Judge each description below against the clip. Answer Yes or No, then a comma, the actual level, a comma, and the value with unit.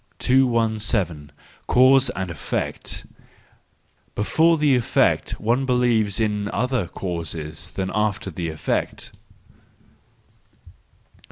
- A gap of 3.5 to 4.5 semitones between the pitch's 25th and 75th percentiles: No, wide, 5.5 semitones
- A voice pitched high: No, low, 110 Hz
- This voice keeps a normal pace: No, slow, 85 wpm